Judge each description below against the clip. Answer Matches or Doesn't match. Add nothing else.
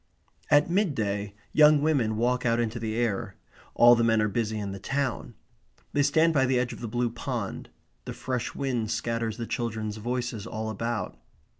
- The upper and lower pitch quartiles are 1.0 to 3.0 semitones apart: Matches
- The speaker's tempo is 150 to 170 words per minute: Doesn't match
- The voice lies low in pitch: Matches